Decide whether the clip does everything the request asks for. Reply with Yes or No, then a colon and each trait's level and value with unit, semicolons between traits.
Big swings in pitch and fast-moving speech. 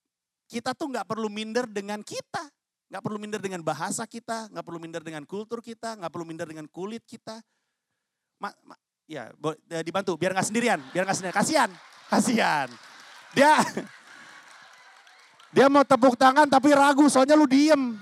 Yes: wide, 6.1 semitones; fast, 155 wpm